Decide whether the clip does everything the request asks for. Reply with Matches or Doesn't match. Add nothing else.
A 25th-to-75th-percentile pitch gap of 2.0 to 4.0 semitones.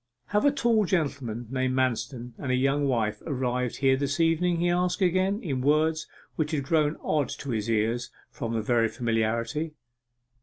Doesn't match